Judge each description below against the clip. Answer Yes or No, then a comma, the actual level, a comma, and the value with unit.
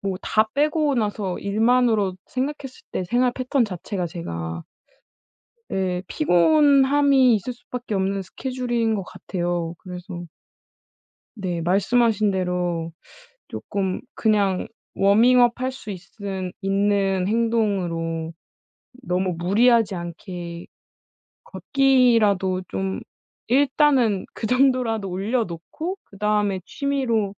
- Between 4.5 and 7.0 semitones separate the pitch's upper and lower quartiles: Yes, average, 5.2 semitones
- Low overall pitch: No, high, 205 Hz